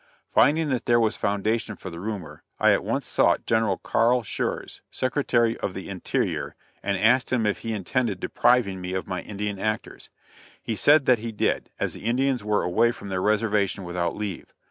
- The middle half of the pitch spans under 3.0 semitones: No, average, 3.3 semitones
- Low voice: Yes, low, 110 Hz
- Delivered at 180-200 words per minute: Yes, average, 190 wpm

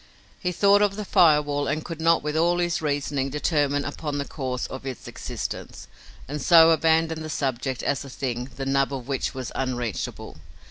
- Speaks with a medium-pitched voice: Yes, medium, 145 Hz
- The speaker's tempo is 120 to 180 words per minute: No, average, 190 wpm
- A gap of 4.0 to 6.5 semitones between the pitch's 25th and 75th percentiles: No, average, 3.3 semitones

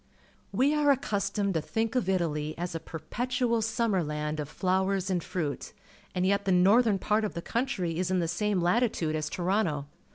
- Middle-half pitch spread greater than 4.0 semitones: Yes, average, 4.8 semitones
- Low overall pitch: No, high, 190 Hz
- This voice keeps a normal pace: Yes, average, 185 wpm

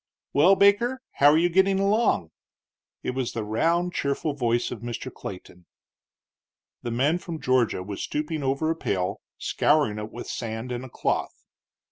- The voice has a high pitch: No, low, 135 Hz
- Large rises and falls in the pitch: Yes, wide, 6.5 semitones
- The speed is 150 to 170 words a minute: Yes, average, 160 wpm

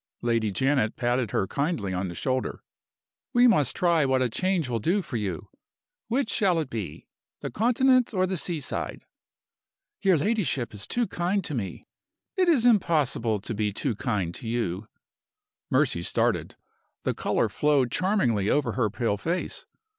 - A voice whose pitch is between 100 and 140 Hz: Yes, low, 135 Hz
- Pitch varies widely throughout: Yes, wide, 9.0 semitones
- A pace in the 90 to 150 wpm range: No, average, 160 wpm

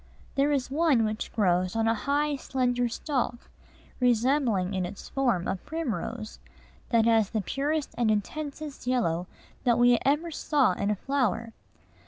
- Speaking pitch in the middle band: No, high, 245 Hz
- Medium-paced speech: Yes, average, 150 wpm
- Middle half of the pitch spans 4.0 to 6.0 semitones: Yes, average, 4.6 semitones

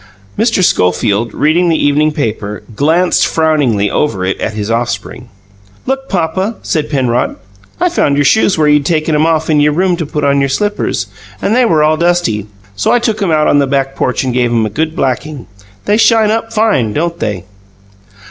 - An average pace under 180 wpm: No, average, 195 wpm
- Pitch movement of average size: No, wide, 6.1 semitones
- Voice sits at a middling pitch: Yes, medium, 150 Hz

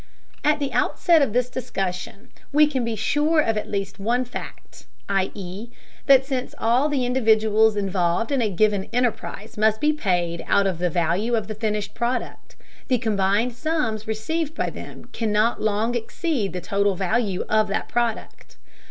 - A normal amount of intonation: Yes, average, 3.8 semitones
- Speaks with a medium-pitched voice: No, high, 220 Hz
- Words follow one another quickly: No, average, 165 wpm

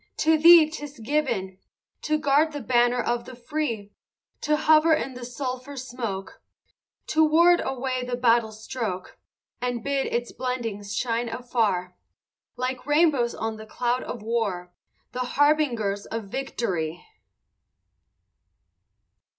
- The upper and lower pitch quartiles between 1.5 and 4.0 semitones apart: No, average, 4.4 semitones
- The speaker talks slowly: Yes, slow, 125 wpm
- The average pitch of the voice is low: No, high, 245 Hz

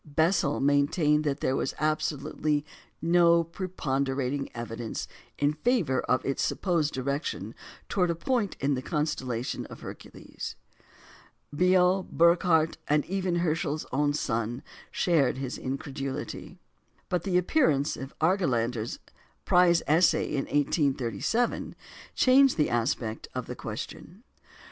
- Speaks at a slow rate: Yes, slow, 110 wpm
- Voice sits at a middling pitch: Yes, medium, 150 Hz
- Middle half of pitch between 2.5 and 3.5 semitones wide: No, average, 4.5 semitones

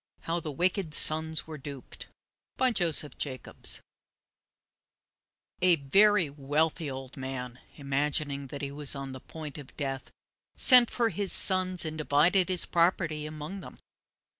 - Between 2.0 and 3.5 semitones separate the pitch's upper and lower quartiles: No, average, 4.1 semitones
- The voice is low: No, medium, 155 Hz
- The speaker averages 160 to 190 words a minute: No, average, 140 wpm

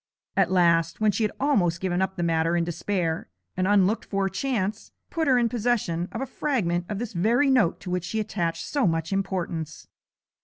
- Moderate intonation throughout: Yes, average, 4.4 semitones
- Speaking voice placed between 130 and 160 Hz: No, high, 190 Hz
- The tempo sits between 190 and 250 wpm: Yes, average, 195 wpm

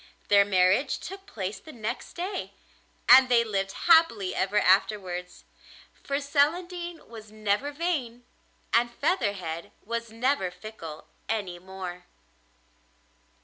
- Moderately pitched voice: No, high, 220 Hz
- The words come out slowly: Yes, slow, 110 wpm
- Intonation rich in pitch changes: Yes, wide, 6.7 semitones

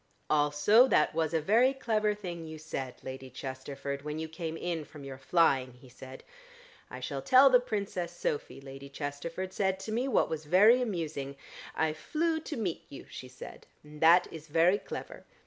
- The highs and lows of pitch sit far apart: Yes, wide, 6.3 semitones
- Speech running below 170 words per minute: No, average, 180 wpm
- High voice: No, medium, 160 Hz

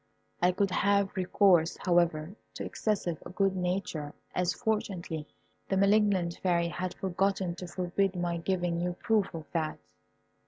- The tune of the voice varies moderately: No, narrow, 2.3 semitones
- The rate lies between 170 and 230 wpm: No, slow, 135 wpm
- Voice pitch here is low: No, medium, 180 Hz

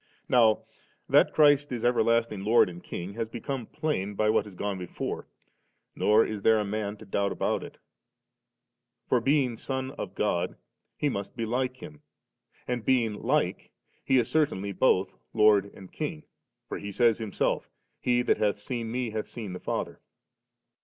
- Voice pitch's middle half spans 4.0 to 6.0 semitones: No, average, 3.6 semitones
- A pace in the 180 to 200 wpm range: No, average, 165 wpm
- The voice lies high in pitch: No, low, 110 Hz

